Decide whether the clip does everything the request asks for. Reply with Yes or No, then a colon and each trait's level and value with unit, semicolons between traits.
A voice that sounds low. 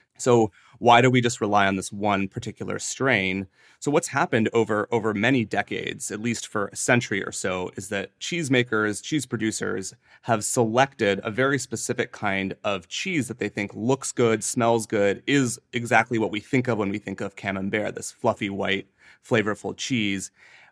Yes: low, 110 Hz